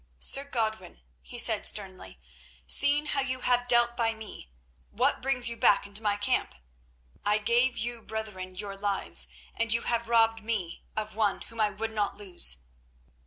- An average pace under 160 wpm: No, average, 165 wpm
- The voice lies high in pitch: Yes, high, 220 Hz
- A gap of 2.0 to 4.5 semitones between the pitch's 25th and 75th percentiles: Yes, average, 2.7 semitones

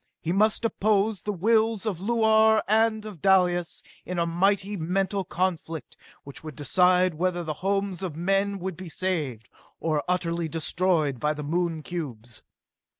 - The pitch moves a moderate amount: Yes, average, 3.5 semitones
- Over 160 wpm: No, average, 150 wpm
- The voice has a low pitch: No, medium, 180 Hz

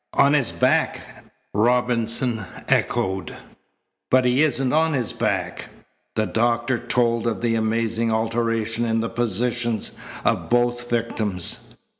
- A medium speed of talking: No, slow, 120 wpm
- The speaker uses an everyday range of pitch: No, narrow, 1.4 semitones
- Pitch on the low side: Yes, low, 115 Hz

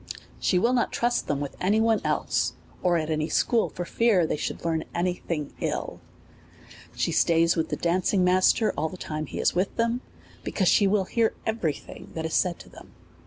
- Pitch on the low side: No, medium, 180 Hz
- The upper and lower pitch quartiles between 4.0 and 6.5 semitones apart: Yes, average, 5.1 semitones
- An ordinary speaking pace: No, fast, 210 wpm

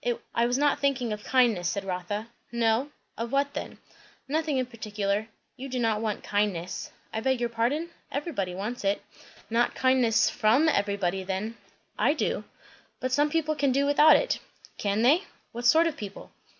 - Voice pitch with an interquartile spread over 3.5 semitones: Yes, average, 5.1 semitones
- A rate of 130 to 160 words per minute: No, average, 170 wpm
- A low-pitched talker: No, high, 235 Hz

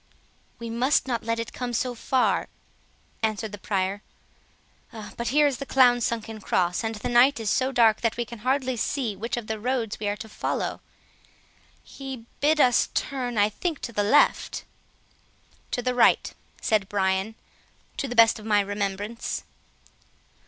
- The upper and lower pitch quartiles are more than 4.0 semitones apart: No, average, 3.1 semitones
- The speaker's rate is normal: Yes, average, 165 wpm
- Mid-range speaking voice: No, high, 230 Hz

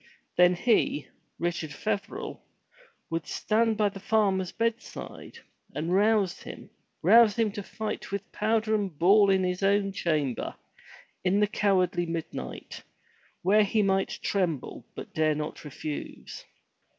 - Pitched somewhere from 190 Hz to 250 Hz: Yes, high, 195 Hz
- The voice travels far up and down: No, average, 3.5 semitones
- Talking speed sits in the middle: No, slow, 130 wpm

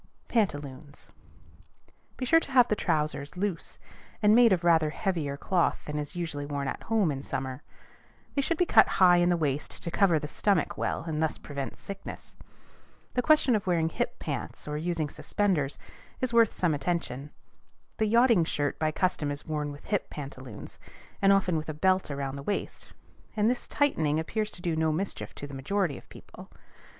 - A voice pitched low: No, medium, 165 Hz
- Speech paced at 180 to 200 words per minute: Yes, average, 185 wpm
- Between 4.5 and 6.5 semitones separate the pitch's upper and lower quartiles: Yes, wide, 5.6 semitones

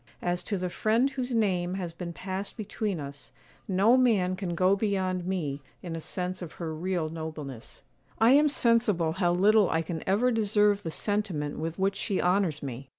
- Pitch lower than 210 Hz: Yes, medium, 185 Hz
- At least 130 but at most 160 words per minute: No, average, 185 wpm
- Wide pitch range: No, average, 4.0 semitones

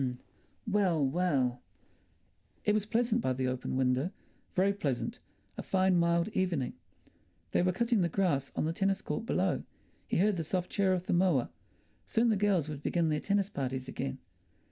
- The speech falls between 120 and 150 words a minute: No, average, 165 wpm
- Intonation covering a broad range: Yes, wide, 6.2 semitones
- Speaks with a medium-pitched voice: Yes, medium, 175 Hz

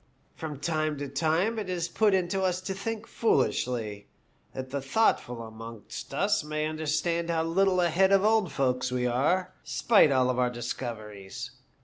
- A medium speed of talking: Yes, average, 165 wpm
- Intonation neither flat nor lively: No, wide, 6.6 semitones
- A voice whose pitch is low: No, medium, 155 Hz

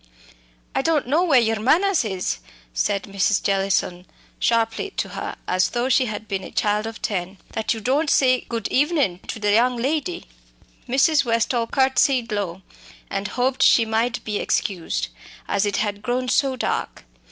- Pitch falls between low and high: No, high, 230 Hz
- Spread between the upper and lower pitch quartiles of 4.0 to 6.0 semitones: Yes, average, 4.4 semitones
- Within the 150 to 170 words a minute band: Yes, average, 165 wpm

